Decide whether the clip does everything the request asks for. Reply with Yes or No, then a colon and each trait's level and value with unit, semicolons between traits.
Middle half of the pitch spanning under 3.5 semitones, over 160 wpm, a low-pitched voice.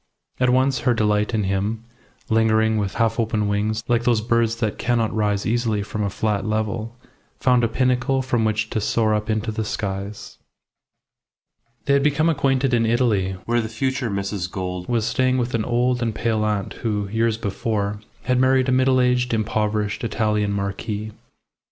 Yes: narrow, 2.6 semitones; average, 175 wpm; low, 110 Hz